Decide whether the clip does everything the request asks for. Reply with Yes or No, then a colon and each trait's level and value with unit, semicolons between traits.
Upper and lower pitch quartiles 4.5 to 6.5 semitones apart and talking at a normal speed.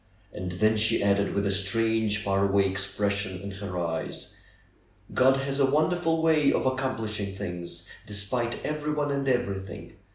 Yes: average, 5.2 semitones; average, 150 wpm